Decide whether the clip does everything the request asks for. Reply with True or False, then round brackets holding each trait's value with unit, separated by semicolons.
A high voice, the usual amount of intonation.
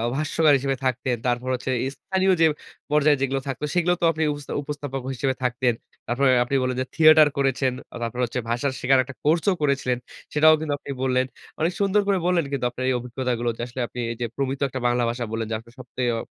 False (135 Hz; 3.2 semitones)